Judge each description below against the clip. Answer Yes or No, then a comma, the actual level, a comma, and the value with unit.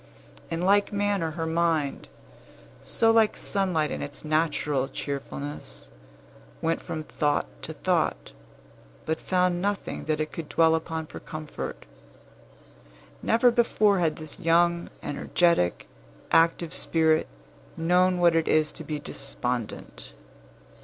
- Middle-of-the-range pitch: Yes, medium, 165 Hz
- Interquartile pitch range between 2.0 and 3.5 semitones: Yes, average, 2.8 semitones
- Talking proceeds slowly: Yes, slow, 120 wpm